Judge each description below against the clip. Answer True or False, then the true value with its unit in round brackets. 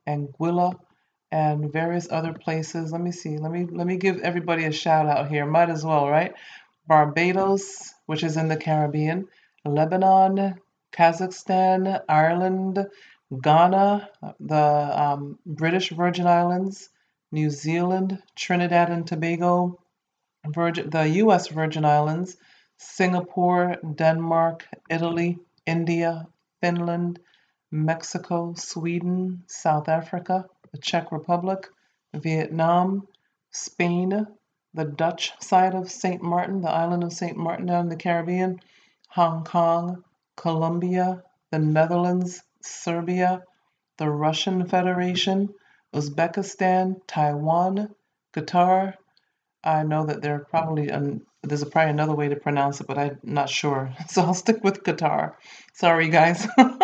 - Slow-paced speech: True (120 wpm)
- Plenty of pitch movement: False (2.7 semitones)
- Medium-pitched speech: True (170 Hz)